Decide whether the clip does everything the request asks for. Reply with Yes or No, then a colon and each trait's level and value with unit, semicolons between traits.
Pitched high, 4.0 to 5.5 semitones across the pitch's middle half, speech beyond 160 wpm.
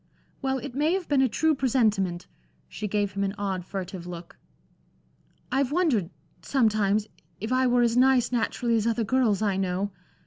Yes: high, 225 Hz; average, 4.8 semitones; average, 170 wpm